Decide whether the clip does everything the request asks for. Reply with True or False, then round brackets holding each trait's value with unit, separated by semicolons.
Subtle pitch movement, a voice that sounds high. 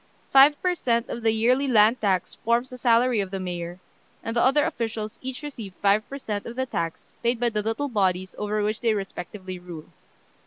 False (3.9 semitones; 225 Hz)